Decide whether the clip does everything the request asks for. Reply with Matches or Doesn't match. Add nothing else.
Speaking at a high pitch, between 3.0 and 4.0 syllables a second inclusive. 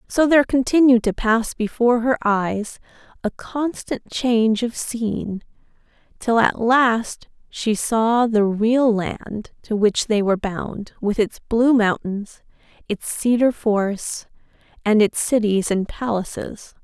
Matches